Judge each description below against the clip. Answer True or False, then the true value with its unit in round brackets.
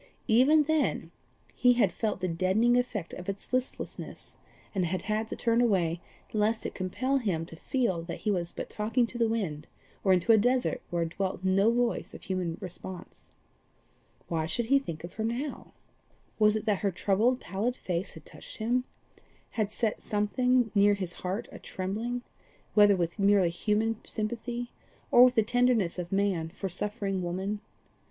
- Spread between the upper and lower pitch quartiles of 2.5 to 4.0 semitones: False (4.4 semitones)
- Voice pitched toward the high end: True (210 Hz)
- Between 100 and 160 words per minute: False (175 wpm)